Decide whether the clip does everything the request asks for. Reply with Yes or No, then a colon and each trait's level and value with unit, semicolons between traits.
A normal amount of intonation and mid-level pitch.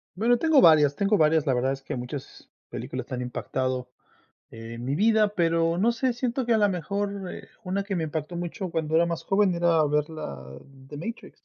No: wide, 6.2 semitones; medium, 165 Hz